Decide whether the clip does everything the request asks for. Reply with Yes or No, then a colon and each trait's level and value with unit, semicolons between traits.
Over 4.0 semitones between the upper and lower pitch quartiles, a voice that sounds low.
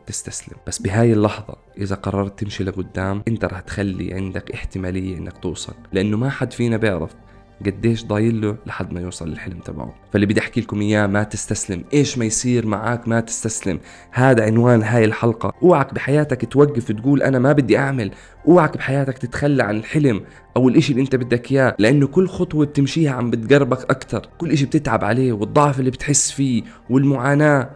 Yes: average, 5.1 semitones; low, 115 Hz